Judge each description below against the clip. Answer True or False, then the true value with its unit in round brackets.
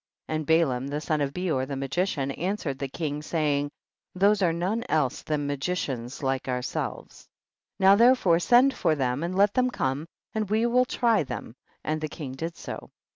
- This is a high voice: False (155 Hz)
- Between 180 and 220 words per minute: True (190 wpm)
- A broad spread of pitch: True (5.8 semitones)